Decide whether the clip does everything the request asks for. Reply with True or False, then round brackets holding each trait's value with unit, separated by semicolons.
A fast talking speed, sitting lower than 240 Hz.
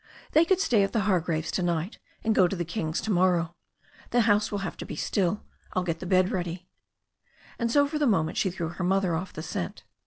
True (235 wpm; 185 Hz)